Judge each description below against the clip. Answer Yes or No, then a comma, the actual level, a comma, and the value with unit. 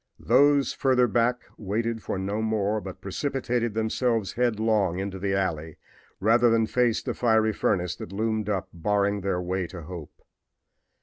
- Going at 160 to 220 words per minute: No, average, 150 wpm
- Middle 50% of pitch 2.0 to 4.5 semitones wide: Yes, average, 3.4 semitones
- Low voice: Yes, low, 110 Hz